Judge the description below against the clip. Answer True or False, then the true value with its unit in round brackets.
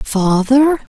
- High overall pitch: True (240 Hz)